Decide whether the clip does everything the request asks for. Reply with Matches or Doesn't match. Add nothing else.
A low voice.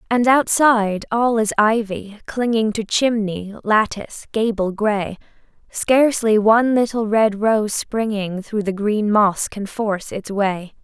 Doesn't match